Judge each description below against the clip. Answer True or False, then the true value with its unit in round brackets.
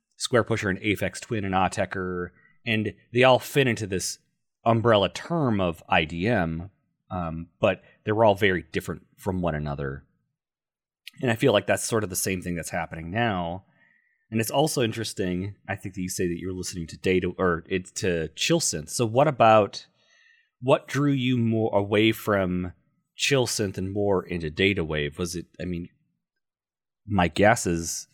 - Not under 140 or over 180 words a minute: True (170 wpm)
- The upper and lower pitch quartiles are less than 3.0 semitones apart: False (4.4 semitones)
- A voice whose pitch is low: True (95 Hz)